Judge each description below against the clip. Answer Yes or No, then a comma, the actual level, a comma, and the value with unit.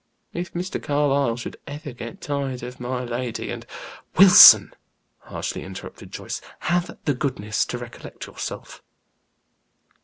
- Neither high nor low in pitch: No, low, 130 Hz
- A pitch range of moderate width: Yes, average, 3.3 semitones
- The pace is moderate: No, slow, 130 wpm